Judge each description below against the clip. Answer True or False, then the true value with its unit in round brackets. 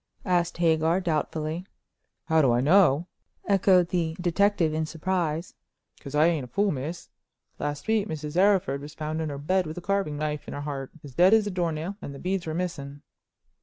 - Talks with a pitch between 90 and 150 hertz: False (160 Hz)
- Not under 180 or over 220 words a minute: True (200 wpm)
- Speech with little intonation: False (3.4 semitones)